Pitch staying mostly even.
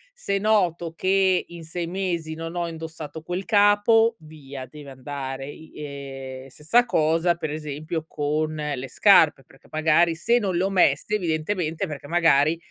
No: average, 3.6 semitones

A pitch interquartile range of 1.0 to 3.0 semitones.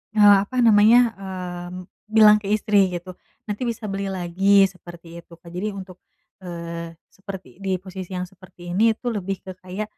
Yes: average, 2.7 semitones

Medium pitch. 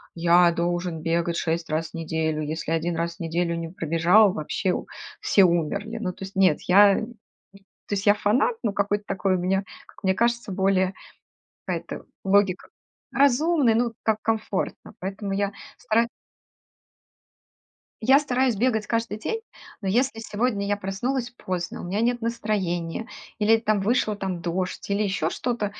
No: high, 200 Hz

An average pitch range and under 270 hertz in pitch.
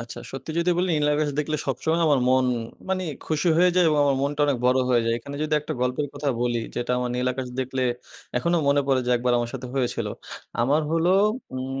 Yes: average, 3.4 semitones; medium, 140 Hz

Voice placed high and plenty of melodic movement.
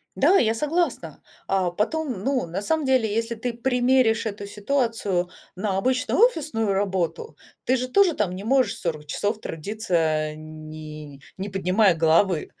Yes: high, 210 Hz; wide, 6.2 semitones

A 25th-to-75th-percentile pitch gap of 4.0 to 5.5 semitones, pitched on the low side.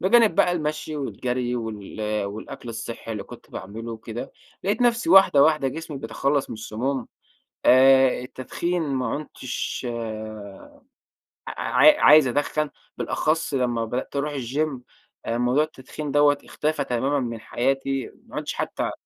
Yes: average, 4.5 semitones; low, 130 Hz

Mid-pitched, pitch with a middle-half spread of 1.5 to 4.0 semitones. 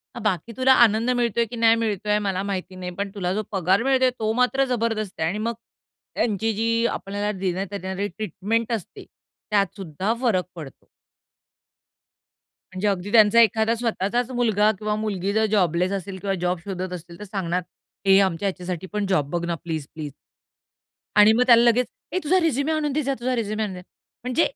No: high, 205 Hz; average, 3.6 semitones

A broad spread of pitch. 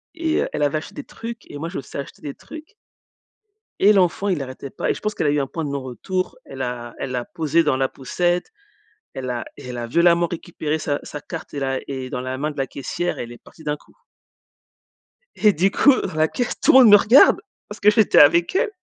Yes: wide, 5.9 semitones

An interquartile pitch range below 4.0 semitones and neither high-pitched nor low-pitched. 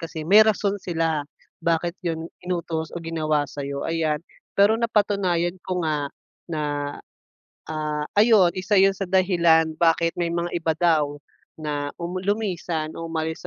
Yes: average, 2.7 semitones; medium, 165 Hz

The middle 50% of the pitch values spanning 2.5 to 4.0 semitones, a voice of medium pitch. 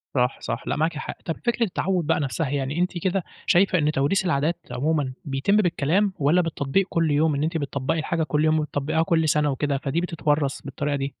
Yes: average, 3.2 semitones; medium, 155 Hz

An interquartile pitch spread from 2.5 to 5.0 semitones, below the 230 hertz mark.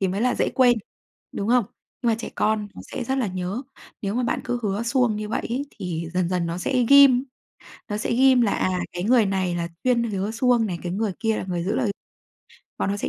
Yes: average, 4.5 semitones; high, 215 Hz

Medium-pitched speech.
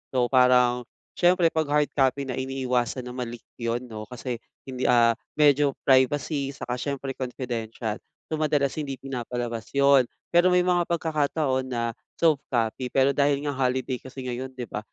No: low, 130 Hz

